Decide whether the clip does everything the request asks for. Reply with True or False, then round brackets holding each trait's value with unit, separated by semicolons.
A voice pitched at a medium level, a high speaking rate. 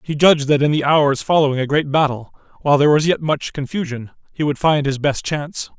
True (145 Hz; 230 wpm)